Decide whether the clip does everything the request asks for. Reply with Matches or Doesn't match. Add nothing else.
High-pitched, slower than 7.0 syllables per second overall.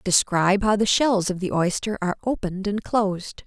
Matches